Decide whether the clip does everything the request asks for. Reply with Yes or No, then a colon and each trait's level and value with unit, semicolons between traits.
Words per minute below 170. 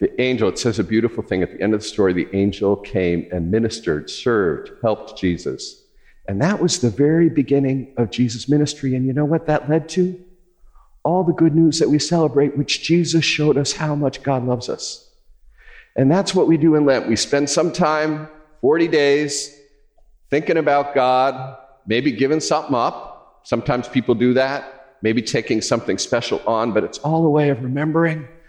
No: average, 185 wpm